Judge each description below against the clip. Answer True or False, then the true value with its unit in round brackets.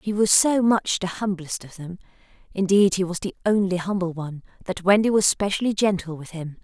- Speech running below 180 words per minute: False (200 wpm)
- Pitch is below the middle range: False (190 Hz)